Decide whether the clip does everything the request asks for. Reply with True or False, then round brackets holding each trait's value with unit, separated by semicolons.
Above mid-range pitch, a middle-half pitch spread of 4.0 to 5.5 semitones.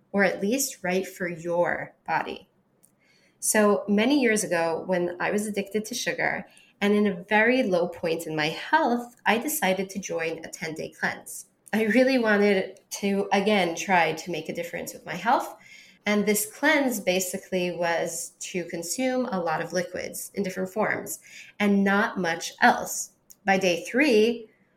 False (195 Hz; 3.5 semitones)